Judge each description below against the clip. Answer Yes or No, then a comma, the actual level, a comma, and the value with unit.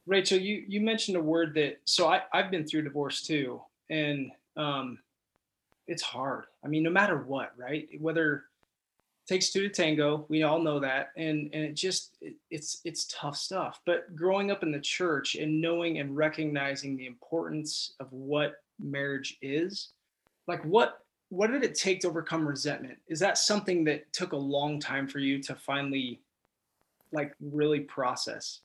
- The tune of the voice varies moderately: Yes, average, 3.4 semitones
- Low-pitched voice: No, medium, 155 Hz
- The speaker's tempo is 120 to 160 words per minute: No, average, 175 wpm